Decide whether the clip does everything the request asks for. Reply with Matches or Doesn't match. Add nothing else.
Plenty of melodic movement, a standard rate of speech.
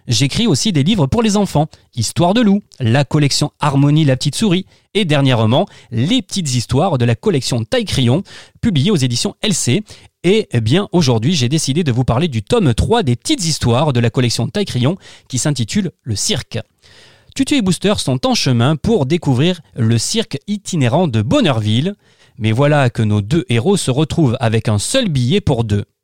Matches